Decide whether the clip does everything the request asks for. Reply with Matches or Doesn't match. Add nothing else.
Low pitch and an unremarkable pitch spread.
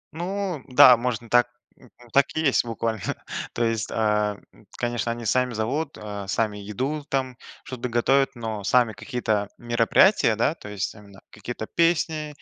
Matches